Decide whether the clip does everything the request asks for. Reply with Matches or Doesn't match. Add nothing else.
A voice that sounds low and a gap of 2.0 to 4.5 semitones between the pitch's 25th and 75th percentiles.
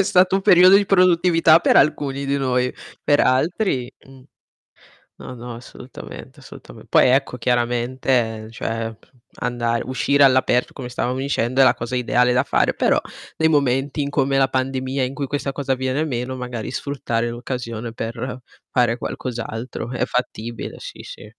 Matches